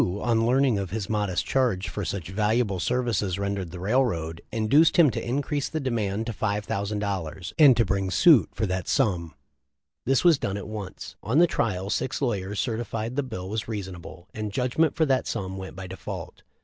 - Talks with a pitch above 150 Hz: No, low, 105 Hz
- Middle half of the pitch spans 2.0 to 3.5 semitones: No, average, 4.6 semitones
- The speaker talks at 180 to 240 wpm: Yes, average, 190 wpm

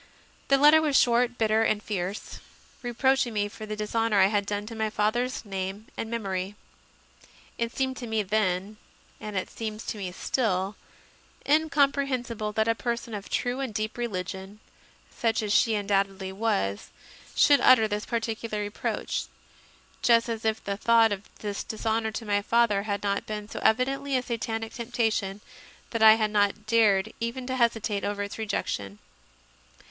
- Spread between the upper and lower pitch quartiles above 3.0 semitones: No, narrow, 2.5 semitones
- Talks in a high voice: Yes, high, 220 Hz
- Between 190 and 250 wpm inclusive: No, average, 165 wpm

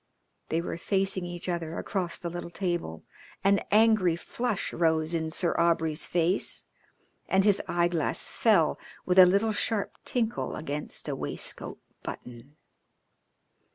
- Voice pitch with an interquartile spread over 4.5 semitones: No, average, 3.1 semitones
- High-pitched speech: No, medium, 175 Hz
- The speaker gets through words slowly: Yes, slow, 130 wpm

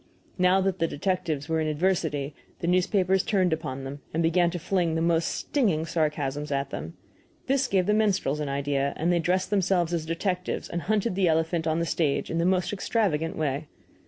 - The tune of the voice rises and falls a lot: No, average, 3.5 semitones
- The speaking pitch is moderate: Yes, medium, 170 Hz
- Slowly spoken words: No, average, 195 wpm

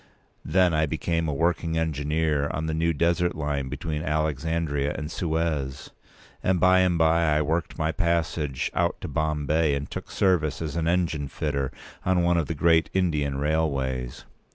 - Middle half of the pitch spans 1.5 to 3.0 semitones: Yes, narrow, 2.4 semitones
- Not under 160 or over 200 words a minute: Yes, average, 165 wpm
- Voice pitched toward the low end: Yes, very low, 80 Hz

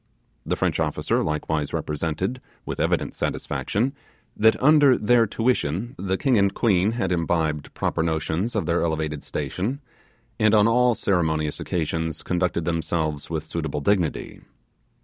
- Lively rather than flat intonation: Yes, wide, 5.7 semitones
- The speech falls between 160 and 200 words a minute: No, slow, 135 wpm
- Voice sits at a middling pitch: No, very low, 90 Hz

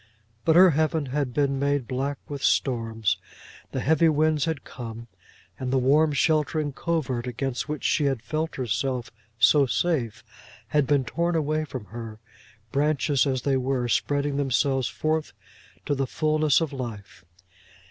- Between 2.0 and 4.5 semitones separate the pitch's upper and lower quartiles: Yes, average, 3.4 semitones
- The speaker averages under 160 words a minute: Yes, average, 150 wpm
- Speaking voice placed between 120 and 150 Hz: Yes, medium, 140 Hz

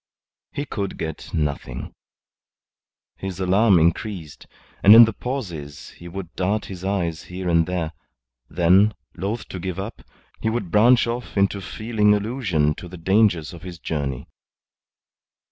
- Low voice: Yes, very low, 95 Hz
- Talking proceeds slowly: No, average, 145 wpm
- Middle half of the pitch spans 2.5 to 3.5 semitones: No, average, 4.0 semitones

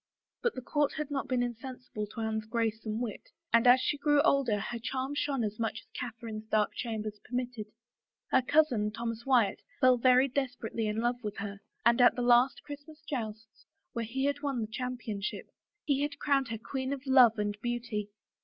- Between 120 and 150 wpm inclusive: No, average, 190 wpm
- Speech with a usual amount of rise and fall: Yes, average, 3.3 semitones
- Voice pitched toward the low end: No, high, 240 Hz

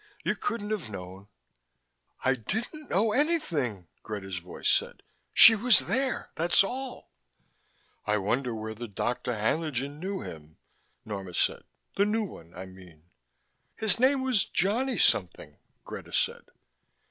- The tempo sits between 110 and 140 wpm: Yes, slow, 135 wpm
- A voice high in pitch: No, medium, 140 Hz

